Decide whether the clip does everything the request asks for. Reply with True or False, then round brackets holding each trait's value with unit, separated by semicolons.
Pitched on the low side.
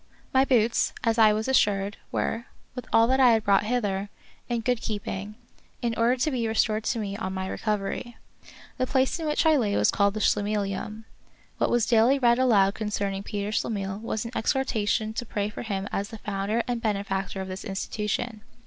False (215 Hz)